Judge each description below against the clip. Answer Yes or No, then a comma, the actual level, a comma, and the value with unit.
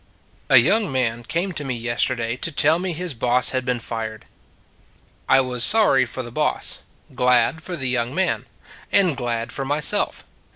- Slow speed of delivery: No, average, 170 wpm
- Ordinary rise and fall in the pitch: Yes, average, 4.9 semitones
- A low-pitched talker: Yes, low, 130 Hz